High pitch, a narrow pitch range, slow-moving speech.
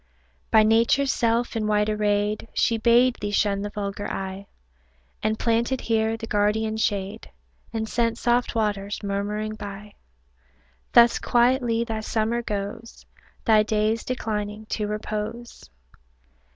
Yes: high, 220 Hz; narrow, 1.8 semitones; slow, 125 wpm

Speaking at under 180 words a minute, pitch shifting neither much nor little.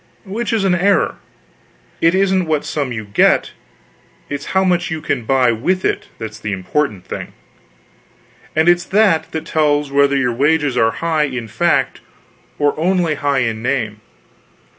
No: average, 160 wpm; wide, 6.0 semitones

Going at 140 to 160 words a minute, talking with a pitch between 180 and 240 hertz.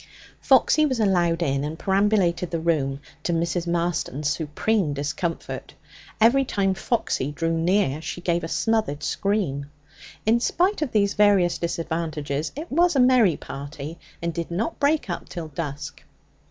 No: average, 150 wpm; medium, 170 Hz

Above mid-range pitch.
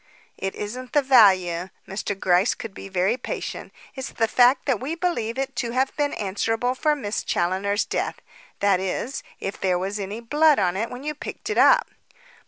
Yes: high, 225 Hz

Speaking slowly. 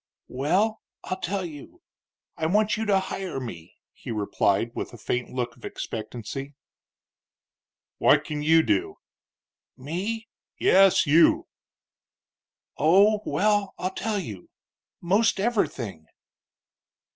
Yes: slow, 110 wpm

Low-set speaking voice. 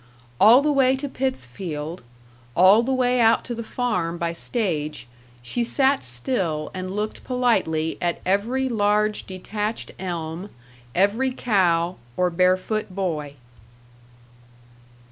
No: high, 195 Hz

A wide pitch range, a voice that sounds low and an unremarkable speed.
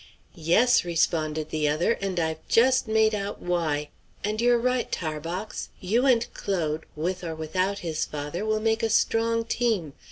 No: wide, 6.0 semitones; medium, 185 Hz; average, 160 wpm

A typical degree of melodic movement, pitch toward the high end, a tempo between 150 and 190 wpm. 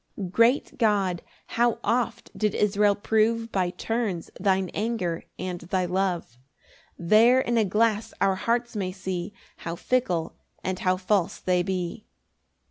No: average, 3.7 semitones; high, 195 Hz; average, 140 wpm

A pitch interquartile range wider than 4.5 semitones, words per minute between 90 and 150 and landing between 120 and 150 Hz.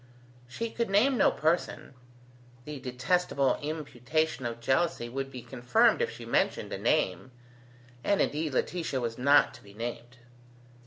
Yes: average, 4.9 semitones; average, 145 wpm; low, 135 Hz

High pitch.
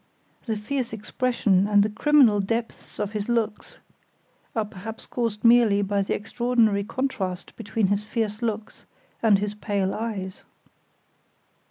Yes: high, 215 Hz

